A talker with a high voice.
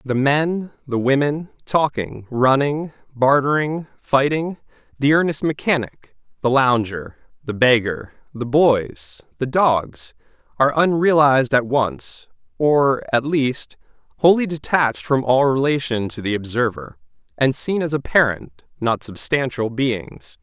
No: low, 130 Hz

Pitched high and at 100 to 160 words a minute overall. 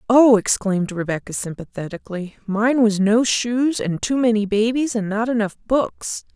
Yes: high, 220 Hz; average, 140 wpm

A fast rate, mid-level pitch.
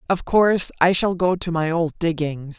Yes: fast, 210 wpm; medium, 170 Hz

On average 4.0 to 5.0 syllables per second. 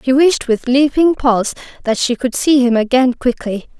Yes: 4.9 syllables/s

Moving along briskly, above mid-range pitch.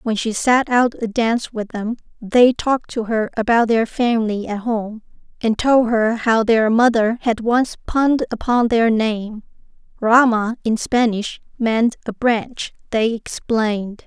No: average, 160 wpm; high, 230 Hz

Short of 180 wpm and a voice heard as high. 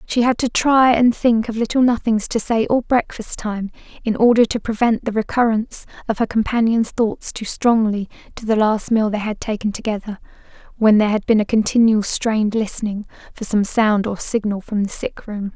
No: average, 195 wpm; high, 220 Hz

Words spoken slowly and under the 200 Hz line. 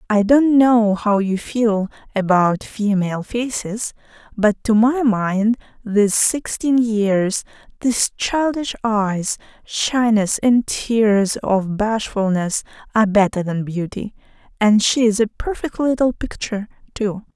No: slow, 125 wpm; high, 215 Hz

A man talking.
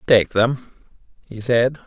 Yes: male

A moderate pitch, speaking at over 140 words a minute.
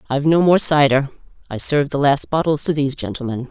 Yes: medium, 145 Hz; fast, 205 wpm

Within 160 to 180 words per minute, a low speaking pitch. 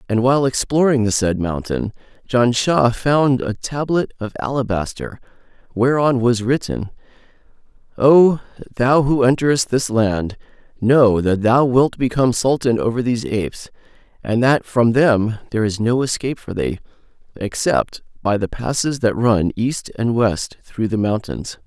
No: average, 145 wpm; low, 120 Hz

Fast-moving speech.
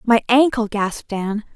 No: average, 155 wpm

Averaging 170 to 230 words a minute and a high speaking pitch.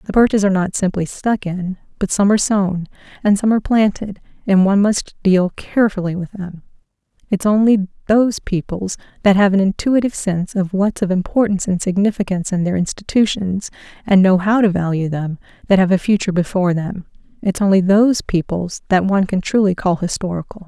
Yes: average, 175 wpm; high, 195 Hz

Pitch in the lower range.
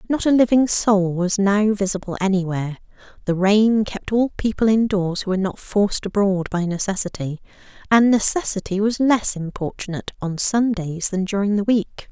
No: high, 200 Hz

